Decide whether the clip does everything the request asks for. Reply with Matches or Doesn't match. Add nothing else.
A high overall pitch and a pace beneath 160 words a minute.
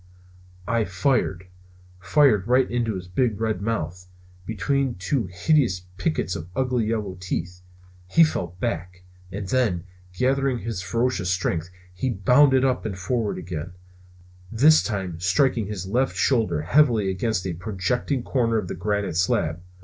Doesn't match